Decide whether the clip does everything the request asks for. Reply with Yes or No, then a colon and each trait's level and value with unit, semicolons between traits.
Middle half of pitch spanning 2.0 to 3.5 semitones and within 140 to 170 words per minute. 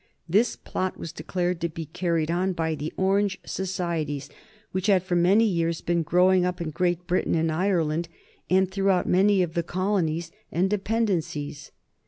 Yes: narrow, 2.4 semitones; average, 165 wpm